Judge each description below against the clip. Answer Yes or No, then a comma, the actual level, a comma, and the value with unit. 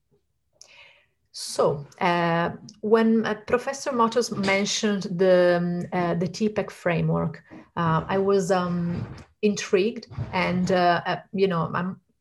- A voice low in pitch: No, high, 190 Hz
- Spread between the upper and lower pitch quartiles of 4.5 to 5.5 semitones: No, average, 3.3 semitones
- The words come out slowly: Yes, slow, 120 wpm